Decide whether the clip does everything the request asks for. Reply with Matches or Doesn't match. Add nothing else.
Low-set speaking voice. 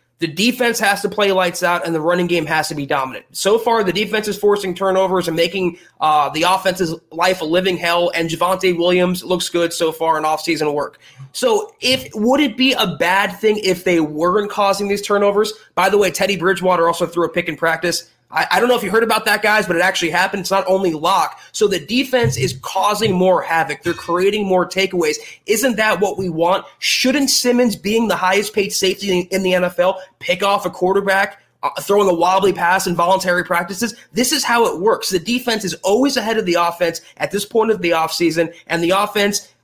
Doesn't match